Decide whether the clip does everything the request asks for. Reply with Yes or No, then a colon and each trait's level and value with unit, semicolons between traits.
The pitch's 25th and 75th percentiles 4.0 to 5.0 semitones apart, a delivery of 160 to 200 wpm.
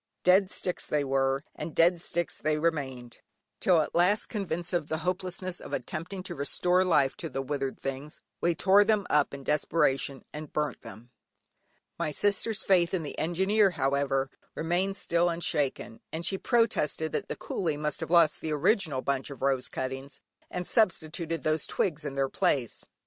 Yes: average, 4.4 semitones; average, 170 wpm